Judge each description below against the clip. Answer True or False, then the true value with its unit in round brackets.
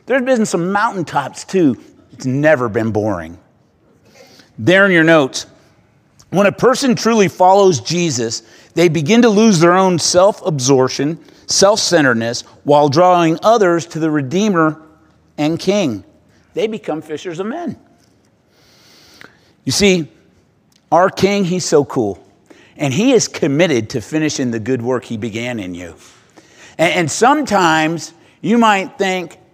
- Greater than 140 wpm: False (135 wpm)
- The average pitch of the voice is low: False (165 Hz)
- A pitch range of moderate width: False (6.7 semitones)